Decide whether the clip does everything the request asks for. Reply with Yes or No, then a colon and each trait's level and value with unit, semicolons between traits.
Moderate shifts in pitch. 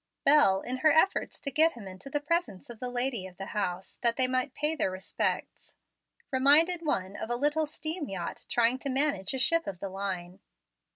No: wide, 7.4 semitones